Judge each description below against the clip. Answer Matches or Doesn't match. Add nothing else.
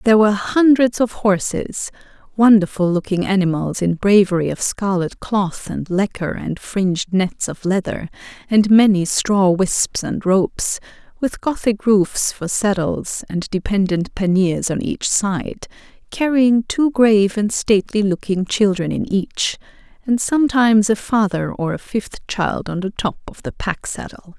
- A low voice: Doesn't match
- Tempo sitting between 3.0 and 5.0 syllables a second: Matches